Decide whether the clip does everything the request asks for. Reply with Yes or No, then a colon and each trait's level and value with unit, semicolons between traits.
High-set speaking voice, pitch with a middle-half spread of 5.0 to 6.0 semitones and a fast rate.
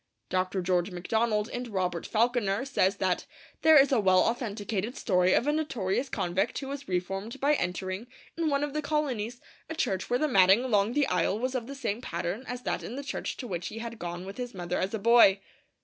Yes: high, 220 Hz; wide, 5.4 semitones; fast, 215 wpm